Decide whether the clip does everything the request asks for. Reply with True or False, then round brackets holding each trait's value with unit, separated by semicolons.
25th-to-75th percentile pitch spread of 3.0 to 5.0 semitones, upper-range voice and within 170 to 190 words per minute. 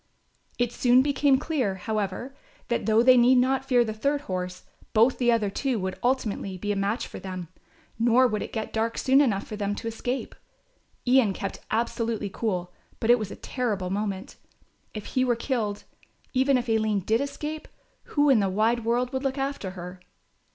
True (4.0 semitones; 230 Hz; 185 wpm)